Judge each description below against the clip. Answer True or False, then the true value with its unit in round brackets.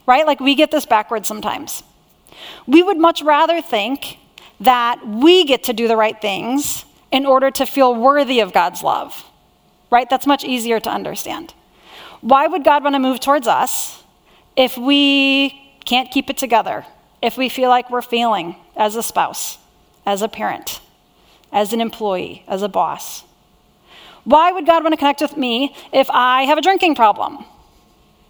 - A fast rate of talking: False (170 wpm)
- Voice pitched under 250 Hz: False (260 Hz)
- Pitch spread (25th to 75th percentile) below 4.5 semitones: True (3.7 semitones)